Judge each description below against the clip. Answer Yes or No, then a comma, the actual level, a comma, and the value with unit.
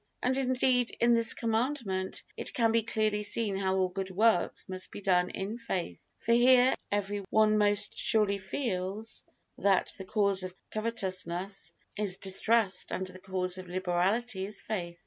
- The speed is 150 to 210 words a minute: Yes, average, 160 wpm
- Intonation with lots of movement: No, average, 3.4 semitones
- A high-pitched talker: Yes, high, 205 Hz